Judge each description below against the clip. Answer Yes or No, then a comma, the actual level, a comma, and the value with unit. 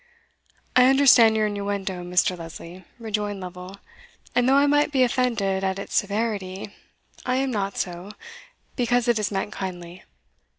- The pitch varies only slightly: No, average, 4.5 semitones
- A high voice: Yes, high, 205 Hz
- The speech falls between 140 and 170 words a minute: Yes, average, 145 wpm